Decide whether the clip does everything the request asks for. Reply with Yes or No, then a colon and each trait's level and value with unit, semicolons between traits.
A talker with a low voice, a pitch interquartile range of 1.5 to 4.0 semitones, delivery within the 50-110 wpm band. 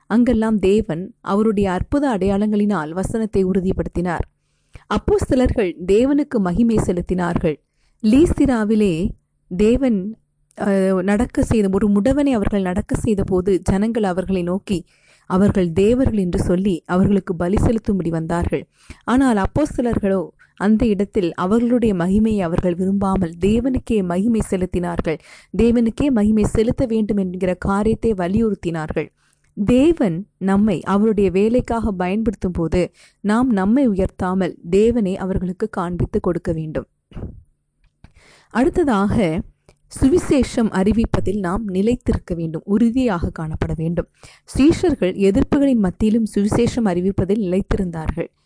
No: high, 200 Hz; average, 3.6 semitones; average, 95 wpm